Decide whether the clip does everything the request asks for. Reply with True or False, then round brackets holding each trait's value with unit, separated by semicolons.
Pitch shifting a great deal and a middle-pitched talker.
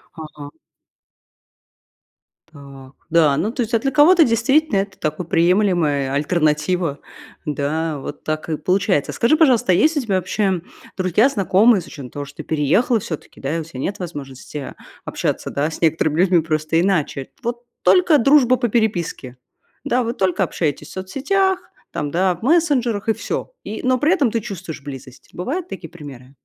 True (7.7 semitones; 180 Hz)